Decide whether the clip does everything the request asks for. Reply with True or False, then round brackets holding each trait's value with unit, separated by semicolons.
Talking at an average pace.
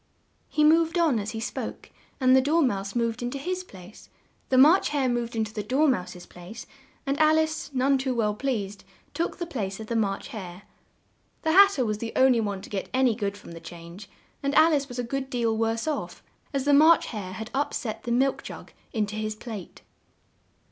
False (225 wpm)